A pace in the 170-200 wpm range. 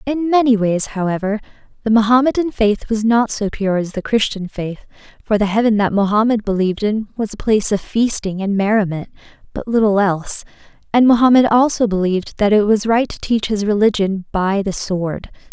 Yes: average, 180 wpm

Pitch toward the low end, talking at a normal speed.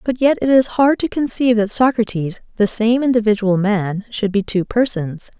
No: high, 220 Hz; average, 190 wpm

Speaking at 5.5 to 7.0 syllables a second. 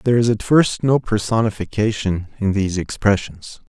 No: 5.3 syllables/s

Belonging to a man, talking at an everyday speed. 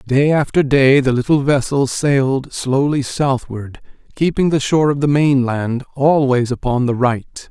Yes: male; average, 150 wpm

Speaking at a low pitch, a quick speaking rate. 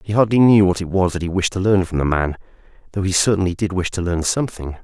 Yes: very low, 95 Hz; fast, 275 wpm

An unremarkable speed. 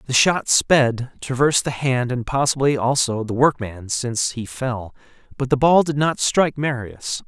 Yes: average, 175 wpm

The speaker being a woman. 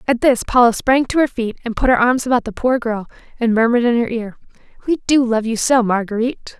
Yes: female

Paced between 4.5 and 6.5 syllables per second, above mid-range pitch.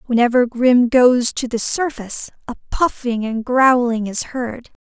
No: 4.2 syllables/s; high, 245 Hz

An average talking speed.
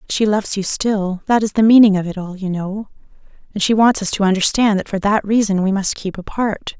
No: fast, 220 wpm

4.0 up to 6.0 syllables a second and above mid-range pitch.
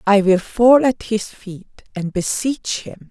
No: 3.5 syllables/s; high, 210 Hz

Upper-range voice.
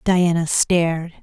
No: medium, 170 Hz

